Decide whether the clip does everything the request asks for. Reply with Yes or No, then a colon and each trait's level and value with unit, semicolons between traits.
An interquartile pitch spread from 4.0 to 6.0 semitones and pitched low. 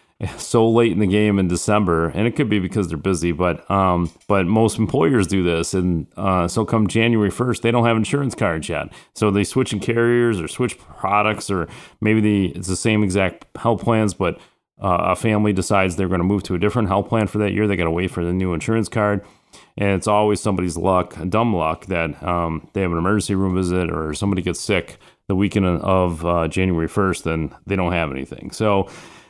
No: average, 3.2 semitones; low, 100 Hz